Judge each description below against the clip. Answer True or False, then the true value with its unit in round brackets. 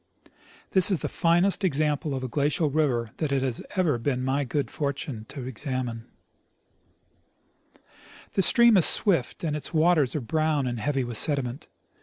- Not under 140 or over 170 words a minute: True (160 wpm)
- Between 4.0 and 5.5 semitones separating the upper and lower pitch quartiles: False (3.6 semitones)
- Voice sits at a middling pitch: True (145 Hz)